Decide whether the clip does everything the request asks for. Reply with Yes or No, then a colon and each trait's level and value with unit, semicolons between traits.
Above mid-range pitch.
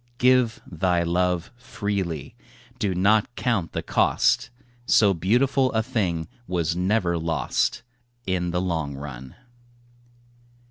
No: very low, 90 Hz